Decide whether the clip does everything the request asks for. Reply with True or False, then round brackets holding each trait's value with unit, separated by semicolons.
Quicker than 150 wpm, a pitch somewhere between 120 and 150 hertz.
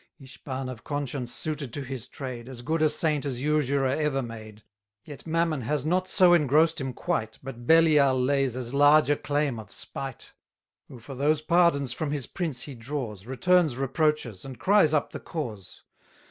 True (175 wpm; 140 Hz)